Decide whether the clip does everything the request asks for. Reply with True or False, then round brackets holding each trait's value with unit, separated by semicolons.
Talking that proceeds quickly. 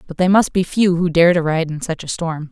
True (310 wpm)